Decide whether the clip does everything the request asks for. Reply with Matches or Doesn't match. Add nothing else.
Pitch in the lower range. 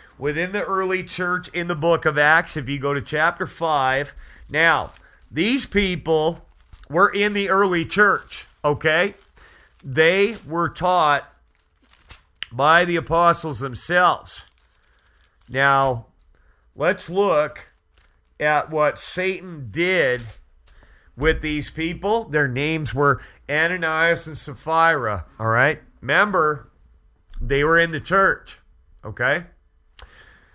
Doesn't match